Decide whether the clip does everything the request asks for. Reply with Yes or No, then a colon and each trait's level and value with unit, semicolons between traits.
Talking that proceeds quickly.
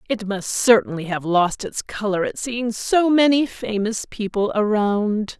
No: average, 155 wpm